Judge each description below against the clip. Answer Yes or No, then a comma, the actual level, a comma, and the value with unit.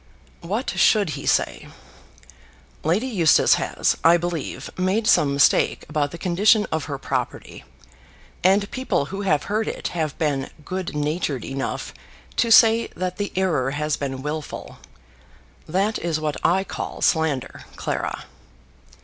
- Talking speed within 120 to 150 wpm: Yes, average, 140 wpm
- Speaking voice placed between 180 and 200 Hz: No, medium, 170 Hz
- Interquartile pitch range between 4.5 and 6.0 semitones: Yes, average, 4.9 semitones